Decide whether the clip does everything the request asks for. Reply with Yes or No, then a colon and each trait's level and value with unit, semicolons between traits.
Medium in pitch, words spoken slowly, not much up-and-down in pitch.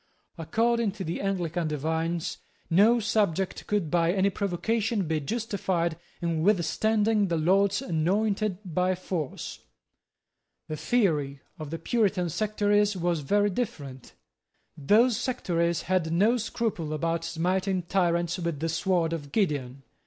No: medium, 180 Hz; slow, 125 wpm; average, 4.0 semitones